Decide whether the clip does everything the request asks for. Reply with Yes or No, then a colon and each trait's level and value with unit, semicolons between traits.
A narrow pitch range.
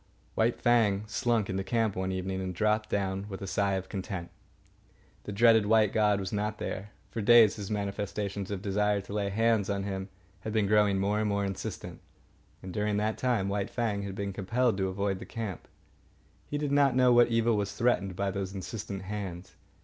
Yes: narrow, 2.2 semitones